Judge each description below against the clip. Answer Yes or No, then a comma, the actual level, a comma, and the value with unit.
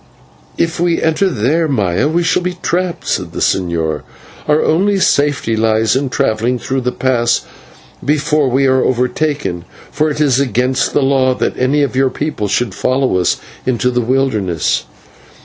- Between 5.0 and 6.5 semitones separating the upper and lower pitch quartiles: No, average, 4.2 semitones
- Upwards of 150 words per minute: Yes, average, 165 wpm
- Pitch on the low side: Yes, low, 130 Hz